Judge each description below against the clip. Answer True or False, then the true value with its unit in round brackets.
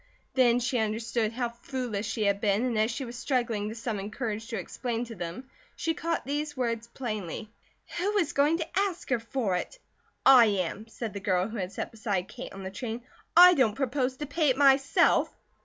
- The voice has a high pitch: True (235 Hz)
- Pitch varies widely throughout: False (4.0 semitones)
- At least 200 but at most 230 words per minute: True (205 wpm)